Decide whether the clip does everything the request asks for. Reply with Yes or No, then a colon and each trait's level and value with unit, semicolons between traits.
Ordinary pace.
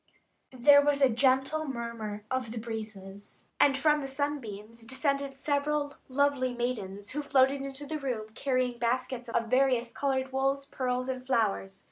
Yes: average, 150 wpm